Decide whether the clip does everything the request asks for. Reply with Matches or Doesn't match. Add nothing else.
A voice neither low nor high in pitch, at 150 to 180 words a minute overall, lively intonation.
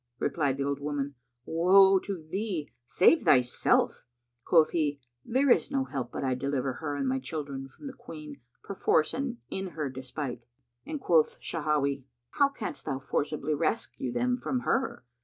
Matches